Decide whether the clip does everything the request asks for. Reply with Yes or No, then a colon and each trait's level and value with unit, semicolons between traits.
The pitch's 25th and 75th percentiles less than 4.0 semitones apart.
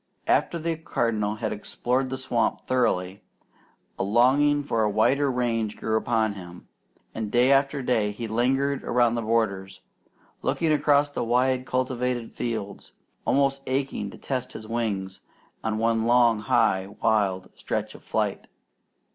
Yes: average, 3.4 semitones